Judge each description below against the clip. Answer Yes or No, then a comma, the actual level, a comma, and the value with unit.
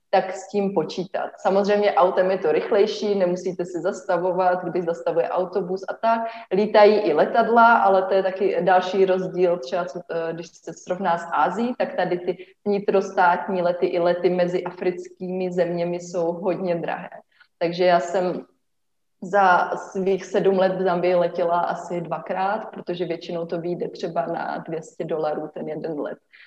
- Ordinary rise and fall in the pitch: No, narrow, 1.7 semitones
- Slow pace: No, average, 155 wpm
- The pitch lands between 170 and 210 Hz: Yes, medium, 185 Hz